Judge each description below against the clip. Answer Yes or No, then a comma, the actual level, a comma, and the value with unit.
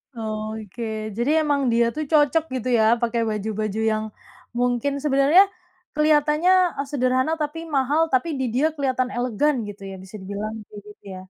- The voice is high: Yes, very high, 250 Hz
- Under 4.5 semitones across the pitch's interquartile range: No, average, 5.3 semitones